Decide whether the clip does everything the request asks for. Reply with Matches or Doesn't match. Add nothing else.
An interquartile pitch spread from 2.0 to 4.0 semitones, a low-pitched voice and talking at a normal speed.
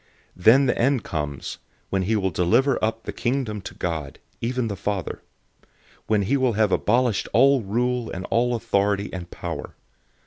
Doesn't match